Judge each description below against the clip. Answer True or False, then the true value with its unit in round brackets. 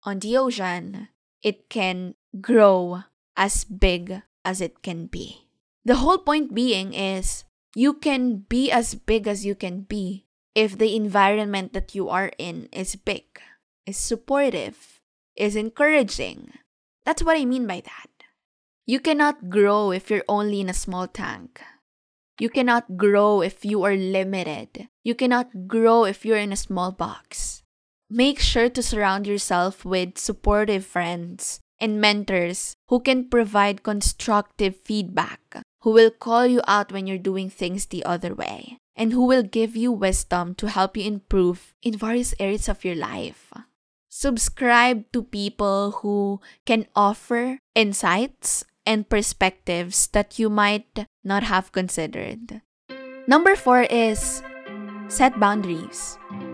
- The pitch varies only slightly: False (3.7 semitones)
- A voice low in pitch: False (210 Hz)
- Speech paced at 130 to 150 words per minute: True (140 wpm)